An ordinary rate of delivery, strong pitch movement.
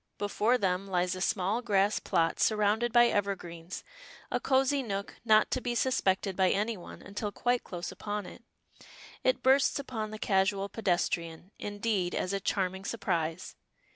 No: average, 155 wpm; average, 3.6 semitones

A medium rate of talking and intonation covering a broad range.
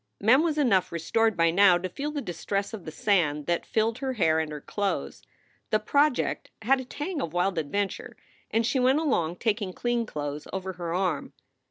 Yes: average, 195 wpm; wide, 6.2 semitones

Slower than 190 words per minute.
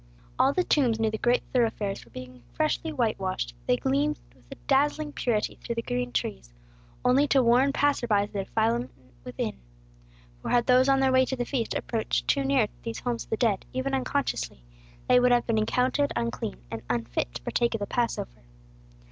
No: average, 200 wpm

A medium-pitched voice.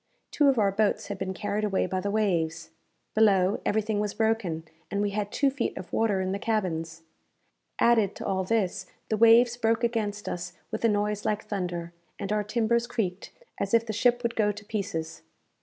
No: high, 210 Hz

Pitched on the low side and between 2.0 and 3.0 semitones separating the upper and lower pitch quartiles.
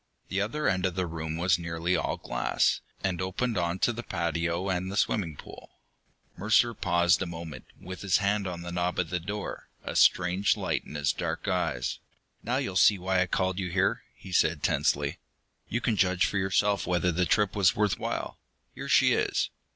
Yes: very low, 90 Hz; narrow, 2.4 semitones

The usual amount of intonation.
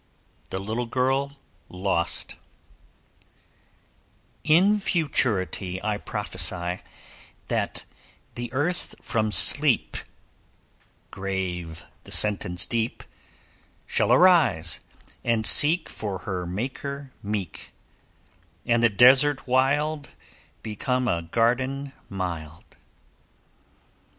No: wide, 6.7 semitones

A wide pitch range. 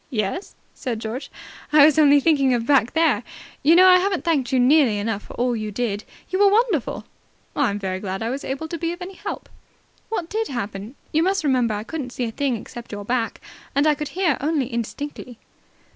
Yes: wide, 5.8 semitones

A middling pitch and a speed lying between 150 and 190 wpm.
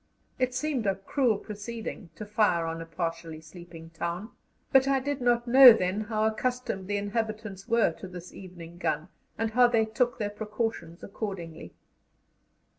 No: high, 210 Hz; average, 160 wpm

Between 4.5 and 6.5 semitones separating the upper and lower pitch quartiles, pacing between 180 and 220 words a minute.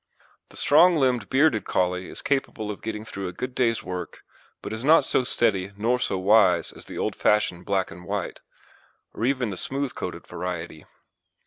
Yes: wide, 5.5 semitones; average, 185 wpm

